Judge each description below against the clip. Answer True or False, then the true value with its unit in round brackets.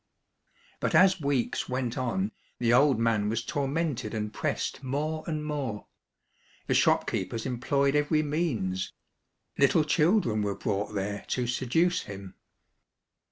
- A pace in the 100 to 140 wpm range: True (135 wpm)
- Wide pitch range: True (5.8 semitones)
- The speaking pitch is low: True (130 Hz)